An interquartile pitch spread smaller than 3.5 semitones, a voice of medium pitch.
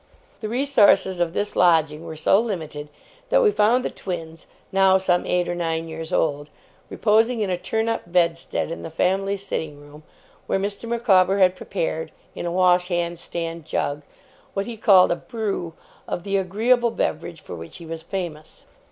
No: average, 3.8 semitones; medium, 180 Hz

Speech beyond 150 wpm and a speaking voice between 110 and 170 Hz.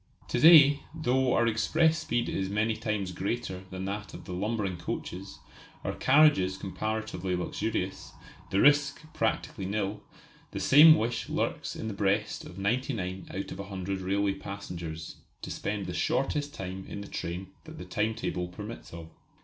No: average, 165 wpm; low, 100 Hz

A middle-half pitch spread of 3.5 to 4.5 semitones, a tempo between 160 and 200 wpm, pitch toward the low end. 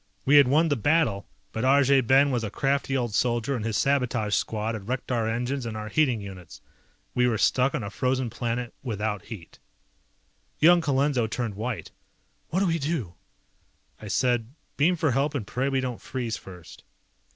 Yes: average, 3.9 semitones; average, 185 wpm; low, 125 Hz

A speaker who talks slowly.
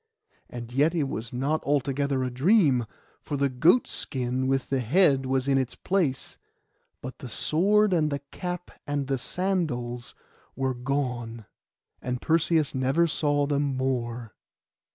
No: average, 145 wpm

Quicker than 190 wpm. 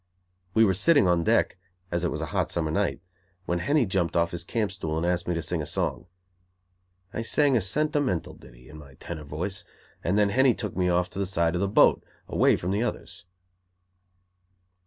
Yes: average, 200 wpm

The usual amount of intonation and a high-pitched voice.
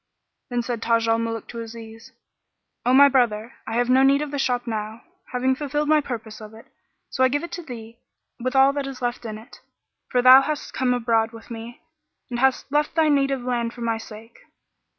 Yes: average, 3.0 semitones; high, 245 Hz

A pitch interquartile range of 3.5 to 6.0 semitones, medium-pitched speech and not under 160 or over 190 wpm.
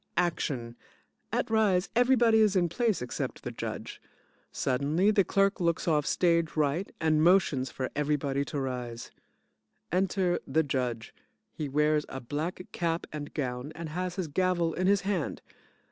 No: average, 4.6 semitones; medium, 165 Hz; average, 150 wpm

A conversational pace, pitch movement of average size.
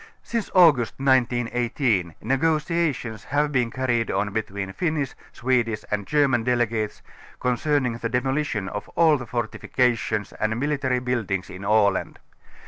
No: slow, 130 wpm; average, 4.0 semitones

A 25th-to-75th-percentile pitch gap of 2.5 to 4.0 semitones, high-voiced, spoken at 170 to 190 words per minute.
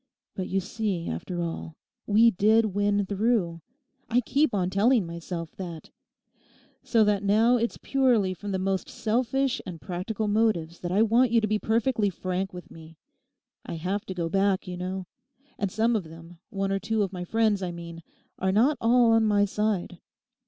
Yes: average, 3.7 semitones; high, 200 Hz; average, 180 wpm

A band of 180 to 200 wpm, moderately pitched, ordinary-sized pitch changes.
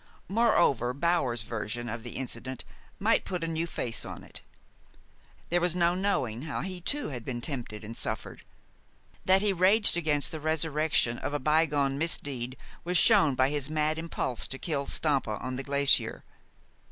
No: average, 165 wpm; medium, 145 Hz; average, 4.9 semitones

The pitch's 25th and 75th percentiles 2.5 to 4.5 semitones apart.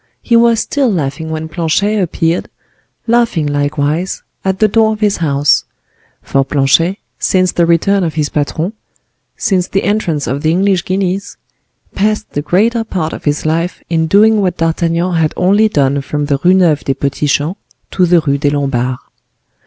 No: average, 5.0 semitones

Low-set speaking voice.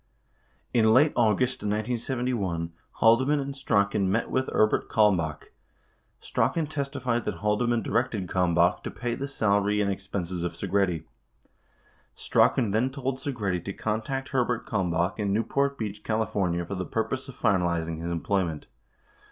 Yes: low, 105 Hz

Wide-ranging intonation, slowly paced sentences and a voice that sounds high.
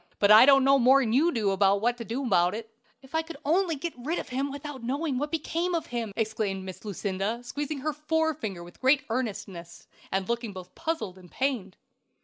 No: wide, 6.2 semitones; fast, 205 wpm; high, 245 Hz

